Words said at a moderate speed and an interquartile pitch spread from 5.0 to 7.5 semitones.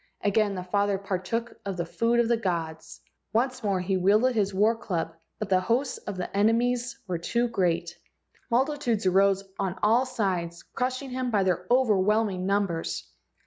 No: average, 180 wpm; average, 4.2 semitones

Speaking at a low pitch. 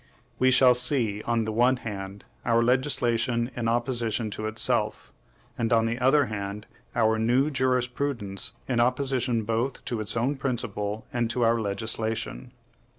Yes: low, 115 Hz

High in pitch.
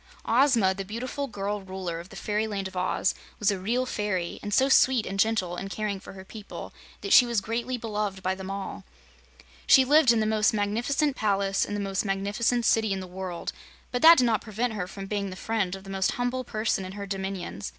Yes: high, 205 Hz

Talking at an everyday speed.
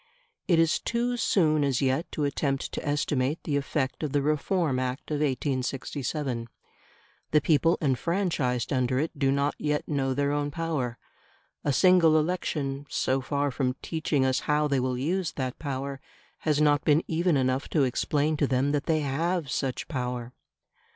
Yes: average, 165 wpm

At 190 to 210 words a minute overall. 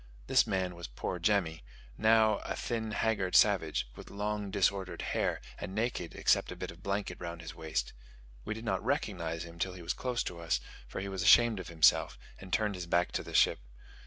Yes: fast, 205 wpm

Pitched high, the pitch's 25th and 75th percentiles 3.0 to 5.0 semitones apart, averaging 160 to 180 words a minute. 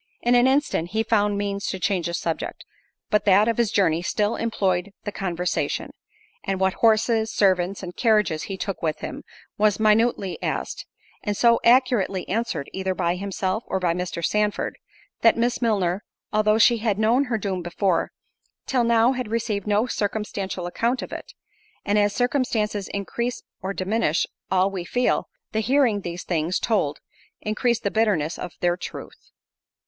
Yes: high, 205 Hz; average, 3.6 semitones; average, 165 wpm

